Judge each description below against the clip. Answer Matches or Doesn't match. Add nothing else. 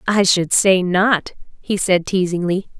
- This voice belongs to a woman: Matches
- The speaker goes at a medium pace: Matches